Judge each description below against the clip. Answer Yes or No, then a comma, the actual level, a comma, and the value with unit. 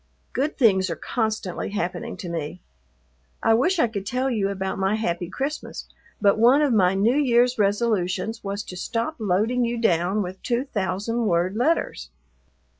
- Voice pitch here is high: Yes, high, 215 Hz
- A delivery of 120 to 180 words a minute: Yes, average, 165 wpm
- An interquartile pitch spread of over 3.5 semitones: Yes, average, 4.1 semitones